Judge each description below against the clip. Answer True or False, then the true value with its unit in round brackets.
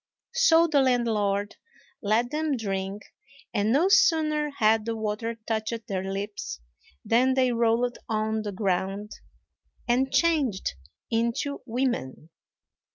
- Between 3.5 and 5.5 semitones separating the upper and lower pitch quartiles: True (4.0 semitones)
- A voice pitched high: True (230 Hz)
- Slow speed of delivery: True (115 wpm)